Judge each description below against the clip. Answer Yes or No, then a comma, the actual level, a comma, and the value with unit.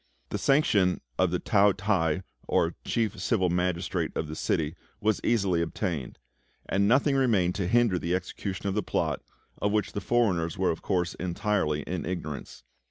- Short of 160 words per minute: No, average, 165 wpm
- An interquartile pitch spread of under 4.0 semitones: Yes, average, 3.4 semitones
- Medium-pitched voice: No, very low, 95 Hz